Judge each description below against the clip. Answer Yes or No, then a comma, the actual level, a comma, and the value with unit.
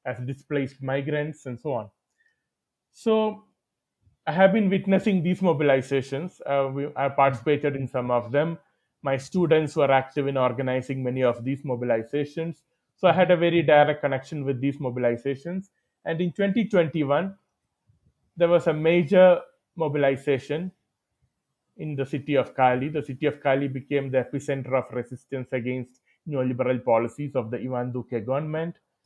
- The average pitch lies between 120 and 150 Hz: Yes, medium, 140 Hz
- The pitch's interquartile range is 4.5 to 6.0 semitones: No, average, 4.1 semitones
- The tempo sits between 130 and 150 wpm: Yes, average, 145 wpm